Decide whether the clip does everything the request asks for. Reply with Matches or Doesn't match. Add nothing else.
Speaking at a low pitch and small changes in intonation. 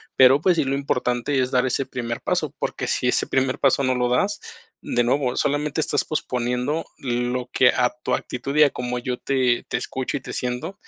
Matches